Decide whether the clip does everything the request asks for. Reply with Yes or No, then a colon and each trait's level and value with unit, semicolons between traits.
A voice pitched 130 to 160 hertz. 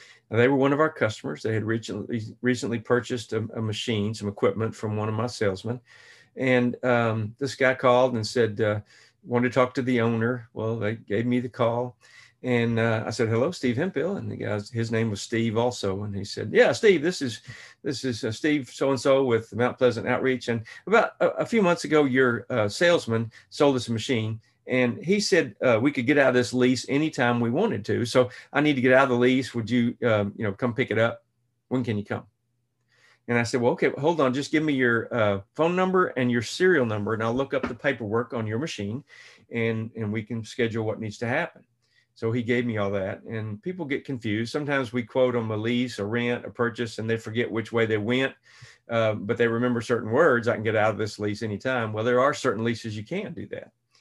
No: low, 120 Hz